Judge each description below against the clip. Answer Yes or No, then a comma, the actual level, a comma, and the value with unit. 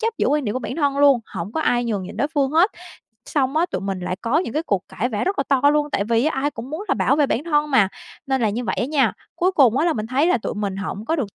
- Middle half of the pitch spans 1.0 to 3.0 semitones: No, average, 5.3 semitones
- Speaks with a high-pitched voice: Yes, very high, 270 Hz